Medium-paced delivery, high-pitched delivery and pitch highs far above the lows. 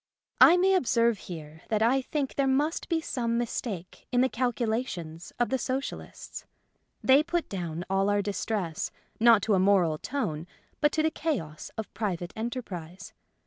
Yes: average, 160 wpm; high, 225 Hz; wide, 6.4 semitones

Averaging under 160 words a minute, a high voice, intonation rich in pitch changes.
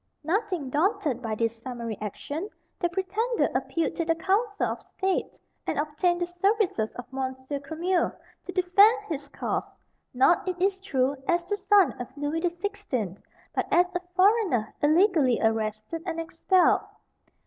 Yes: average, 150 wpm; very high, 340 Hz; wide, 6.5 semitones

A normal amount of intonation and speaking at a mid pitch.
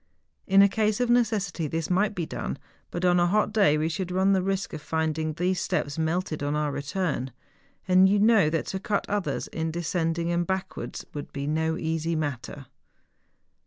Yes: average, 3.5 semitones; medium, 175 Hz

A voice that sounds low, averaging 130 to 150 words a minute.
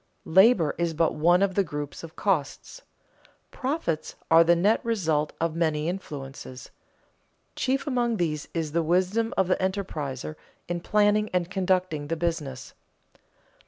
No: medium, 170 Hz; average, 140 wpm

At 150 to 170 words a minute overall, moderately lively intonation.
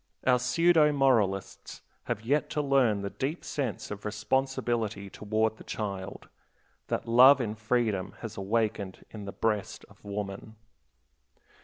No: slow, 135 wpm; average, 4.2 semitones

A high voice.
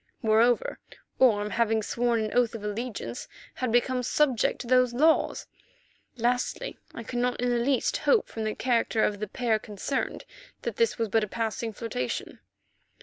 Yes: high, 235 Hz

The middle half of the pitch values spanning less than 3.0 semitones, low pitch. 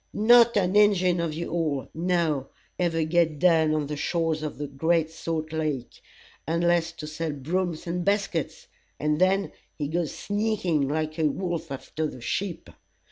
No: narrow, 2.5 semitones; medium, 165 Hz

